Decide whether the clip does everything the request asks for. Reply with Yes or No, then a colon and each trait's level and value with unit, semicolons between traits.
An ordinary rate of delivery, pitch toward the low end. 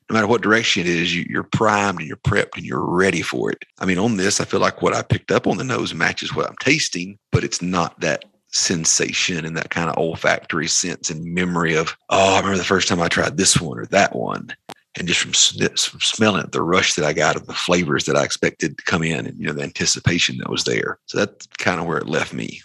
No: fast, 260 wpm; very low, 90 Hz